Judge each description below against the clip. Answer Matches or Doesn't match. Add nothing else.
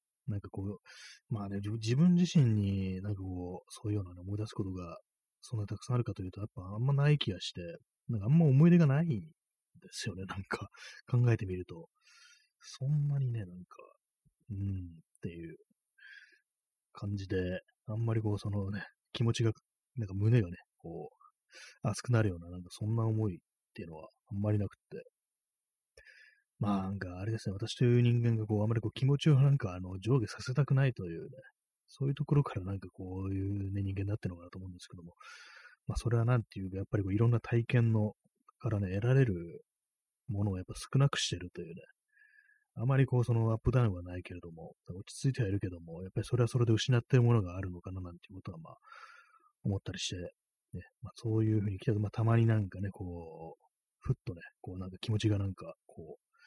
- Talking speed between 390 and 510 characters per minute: Matches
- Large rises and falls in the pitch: Doesn't match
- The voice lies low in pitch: Matches